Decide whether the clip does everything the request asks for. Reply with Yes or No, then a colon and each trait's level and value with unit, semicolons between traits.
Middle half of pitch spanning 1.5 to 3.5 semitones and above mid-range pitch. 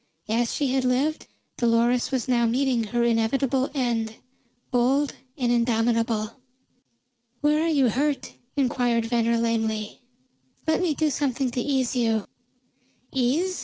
Yes: average, 2.9 semitones; high, 245 Hz